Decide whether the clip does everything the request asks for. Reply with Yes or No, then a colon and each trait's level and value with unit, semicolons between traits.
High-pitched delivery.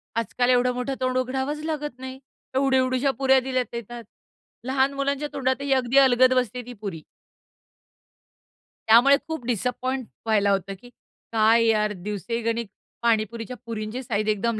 Yes: very high, 250 Hz